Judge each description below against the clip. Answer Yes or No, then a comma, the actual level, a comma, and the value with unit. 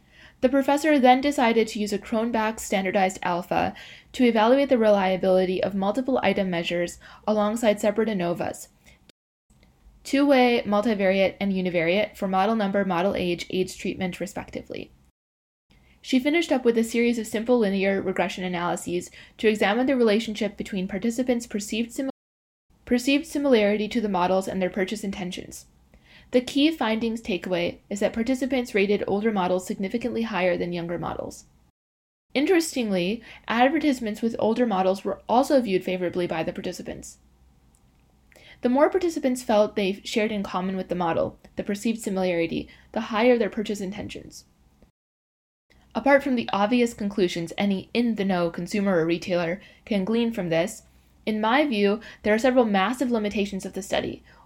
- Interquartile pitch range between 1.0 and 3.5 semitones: No, average, 4.4 semitones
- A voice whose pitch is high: Yes, high, 205 Hz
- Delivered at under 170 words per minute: Yes, average, 150 wpm